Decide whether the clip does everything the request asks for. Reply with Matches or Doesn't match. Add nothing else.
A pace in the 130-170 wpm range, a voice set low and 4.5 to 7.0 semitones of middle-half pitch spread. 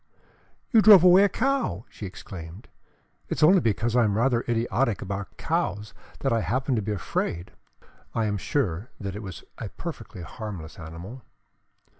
Matches